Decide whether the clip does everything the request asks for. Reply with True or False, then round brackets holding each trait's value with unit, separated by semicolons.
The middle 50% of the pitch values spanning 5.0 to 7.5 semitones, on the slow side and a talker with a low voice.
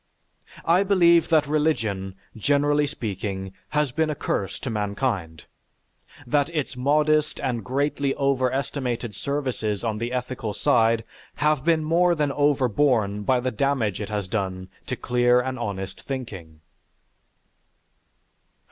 True (5.6 semitones; 125 wpm; 130 Hz)